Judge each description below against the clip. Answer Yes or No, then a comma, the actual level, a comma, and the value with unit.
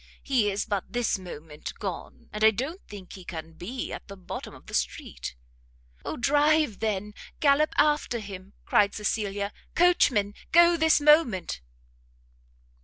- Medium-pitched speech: No, high, 210 Hz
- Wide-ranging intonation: Yes, wide, 7.0 semitones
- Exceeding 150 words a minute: No, average, 145 wpm